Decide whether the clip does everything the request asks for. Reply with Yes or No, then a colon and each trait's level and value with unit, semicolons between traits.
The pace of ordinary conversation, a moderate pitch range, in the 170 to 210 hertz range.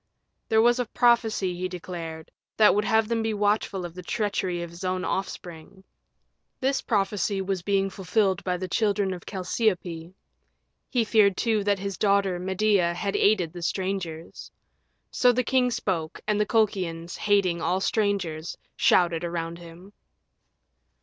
Yes: average, 150 wpm; average, 3.3 semitones; high, 190 Hz